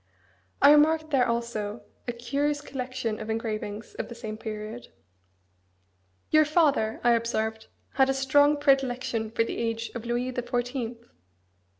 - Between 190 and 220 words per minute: No, average, 140 wpm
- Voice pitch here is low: No, high, 240 Hz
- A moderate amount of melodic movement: Yes, average, 3.1 semitones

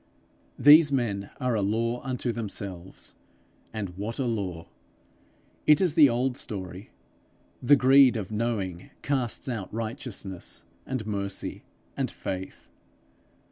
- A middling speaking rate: No, slow, 120 wpm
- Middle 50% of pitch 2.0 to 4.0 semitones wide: No, average, 4.6 semitones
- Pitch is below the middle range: Yes, low, 115 Hz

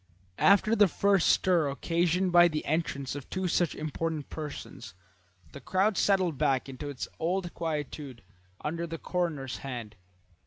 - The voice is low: No, medium, 165 Hz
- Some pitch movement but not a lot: Yes, average, 4.1 semitones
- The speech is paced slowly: No, average, 145 wpm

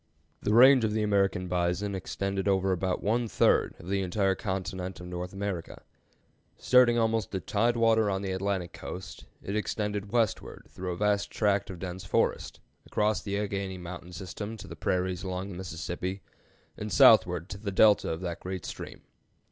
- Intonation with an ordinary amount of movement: No, narrow, 2.3 semitones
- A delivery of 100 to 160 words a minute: No, average, 175 wpm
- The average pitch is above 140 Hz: No, very low, 95 Hz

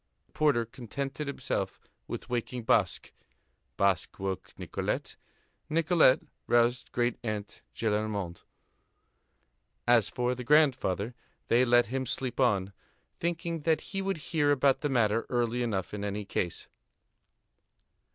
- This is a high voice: No, low, 120 Hz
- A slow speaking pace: Yes, slow, 120 wpm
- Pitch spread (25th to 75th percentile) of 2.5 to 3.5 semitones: No, average, 5.0 semitones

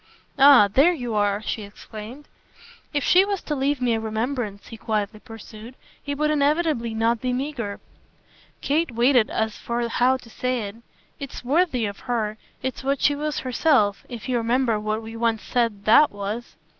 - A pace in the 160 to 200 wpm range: Yes, average, 175 wpm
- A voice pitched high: Yes, high, 240 Hz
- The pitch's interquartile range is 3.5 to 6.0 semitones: Yes, average, 4.2 semitones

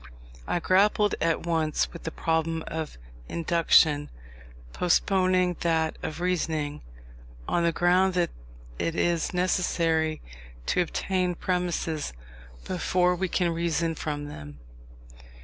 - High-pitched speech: No, medium, 170 Hz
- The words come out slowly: Yes, slow, 115 wpm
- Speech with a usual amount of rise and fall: No, narrow, 2.0 semitones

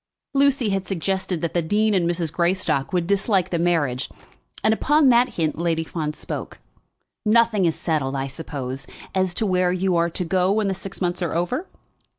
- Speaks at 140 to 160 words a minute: No, average, 185 wpm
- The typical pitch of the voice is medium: Yes, medium, 180 Hz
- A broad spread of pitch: No, average, 3.3 semitones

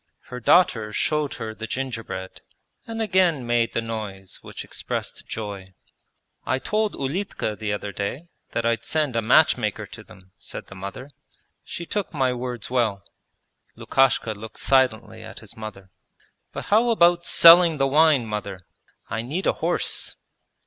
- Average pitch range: No, wide, 6.3 semitones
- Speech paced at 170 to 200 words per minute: No, average, 150 wpm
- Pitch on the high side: No, low, 120 Hz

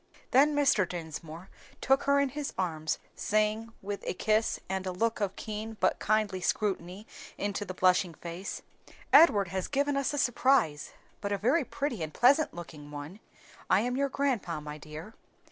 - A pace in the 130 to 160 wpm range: No, average, 170 wpm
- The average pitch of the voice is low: No, high, 205 Hz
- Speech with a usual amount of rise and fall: No, wide, 6.6 semitones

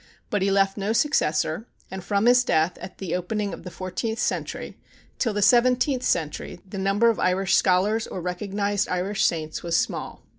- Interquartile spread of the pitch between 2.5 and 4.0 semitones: Yes, average, 3.3 semitones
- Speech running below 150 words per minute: No, average, 180 wpm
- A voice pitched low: No, high, 195 Hz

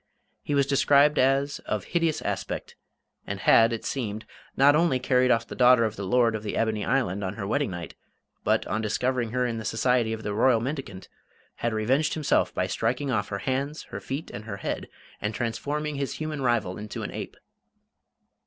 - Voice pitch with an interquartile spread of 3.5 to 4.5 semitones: Yes, average, 4.2 semitones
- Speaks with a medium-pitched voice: No, low, 125 Hz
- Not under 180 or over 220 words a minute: Yes, average, 195 wpm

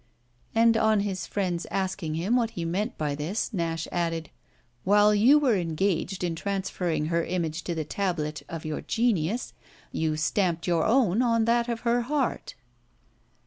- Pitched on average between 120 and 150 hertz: No, medium, 185 Hz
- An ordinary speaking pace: Yes, average, 160 wpm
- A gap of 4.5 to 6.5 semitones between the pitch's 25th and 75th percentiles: Yes, average, 5.2 semitones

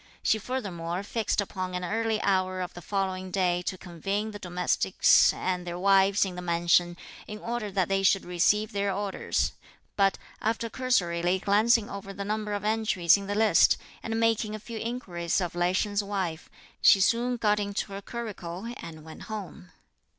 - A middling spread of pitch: Yes, average, 3.1 semitones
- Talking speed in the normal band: Yes, average, 175 wpm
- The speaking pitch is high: Yes, high, 195 Hz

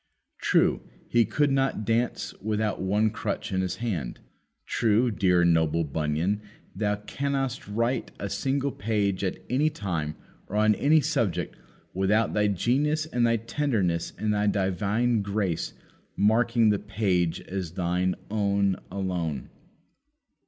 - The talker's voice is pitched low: Yes, low, 105 Hz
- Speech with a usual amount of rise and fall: Yes, average, 3.9 semitones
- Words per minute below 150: Yes, average, 140 wpm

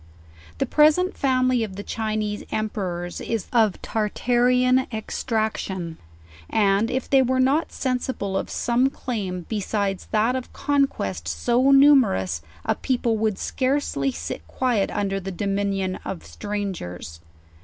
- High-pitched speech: Yes, high, 215 Hz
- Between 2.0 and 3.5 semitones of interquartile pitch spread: No, average, 4.8 semitones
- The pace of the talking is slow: Yes, slow, 130 wpm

